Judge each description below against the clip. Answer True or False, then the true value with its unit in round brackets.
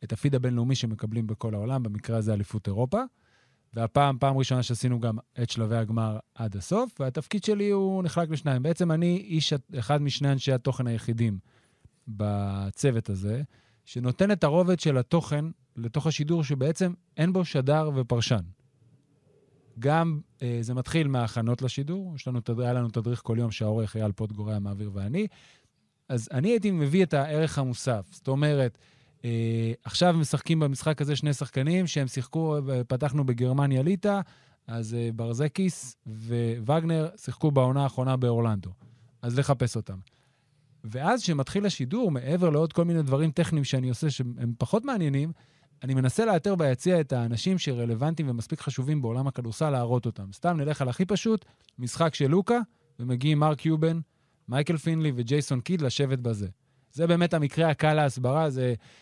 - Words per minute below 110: False (150 wpm)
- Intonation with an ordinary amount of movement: True (5.0 semitones)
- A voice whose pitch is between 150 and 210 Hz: False (135 Hz)